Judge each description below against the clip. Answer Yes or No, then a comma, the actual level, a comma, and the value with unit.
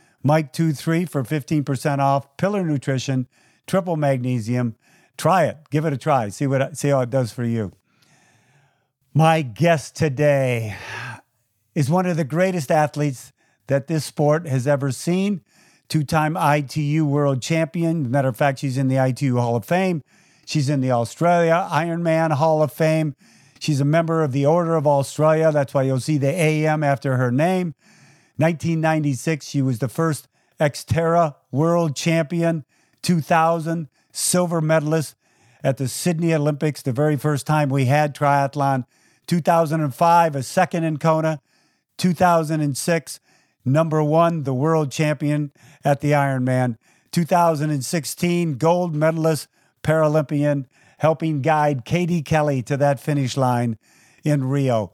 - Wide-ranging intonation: No, average, 3.0 semitones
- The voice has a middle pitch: Yes, medium, 150 Hz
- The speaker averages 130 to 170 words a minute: Yes, average, 140 wpm